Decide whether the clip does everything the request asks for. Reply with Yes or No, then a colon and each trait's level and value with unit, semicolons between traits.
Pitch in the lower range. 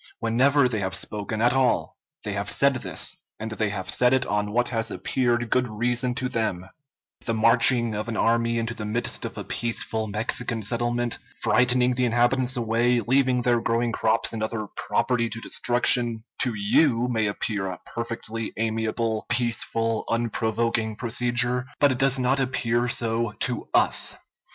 Yes: low, 115 Hz